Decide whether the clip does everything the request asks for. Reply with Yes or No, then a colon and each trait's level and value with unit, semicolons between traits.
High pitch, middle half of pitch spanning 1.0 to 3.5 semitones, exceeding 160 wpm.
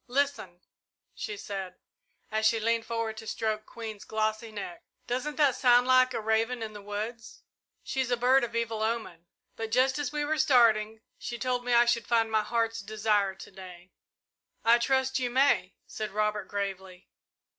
Yes: high, 225 Hz; average, 2.8 semitones; average, 175 wpm